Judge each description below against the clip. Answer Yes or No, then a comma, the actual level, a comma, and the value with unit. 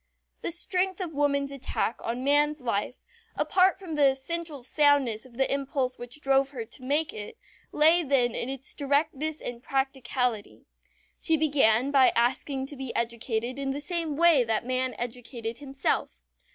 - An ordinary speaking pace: Yes, average, 160 wpm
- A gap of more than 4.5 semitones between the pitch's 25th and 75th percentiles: No, average, 3.2 semitones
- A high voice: Yes, very high, 270 Hz